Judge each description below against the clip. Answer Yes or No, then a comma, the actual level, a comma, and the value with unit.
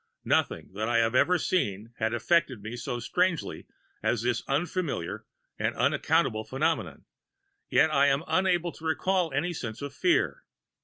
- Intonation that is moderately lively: No, wide, 6.9 semitones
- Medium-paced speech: Yes, average, 150 wpm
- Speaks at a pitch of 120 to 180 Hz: Yes, medium, 140 Hz